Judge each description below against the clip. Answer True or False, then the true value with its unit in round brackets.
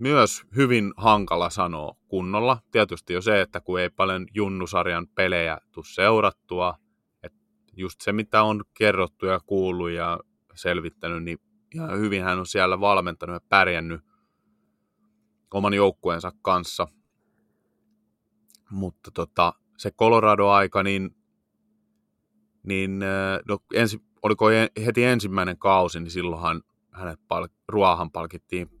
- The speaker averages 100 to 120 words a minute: True (115 wpm)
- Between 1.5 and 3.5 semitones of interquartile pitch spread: True (3.2 semitones)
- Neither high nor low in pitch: False (95 Hz)